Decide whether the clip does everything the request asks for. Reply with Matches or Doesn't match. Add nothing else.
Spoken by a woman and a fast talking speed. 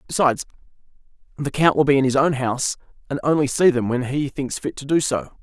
Doesn't match